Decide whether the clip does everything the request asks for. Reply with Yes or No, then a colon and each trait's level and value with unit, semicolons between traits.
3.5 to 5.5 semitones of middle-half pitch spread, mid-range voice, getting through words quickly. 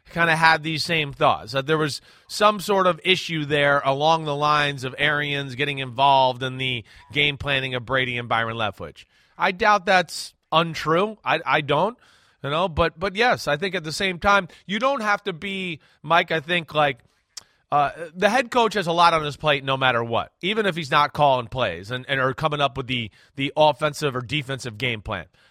Yes: average, 4.5 semitones; medium, 150 Hz; fast, 210 wpm